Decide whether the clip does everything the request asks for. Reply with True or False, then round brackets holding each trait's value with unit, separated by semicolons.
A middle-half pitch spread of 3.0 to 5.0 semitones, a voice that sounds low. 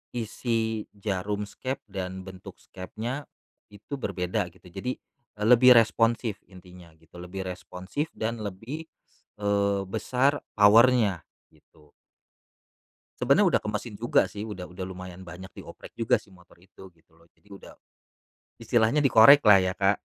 True (3.7 semitones; 100 Hz)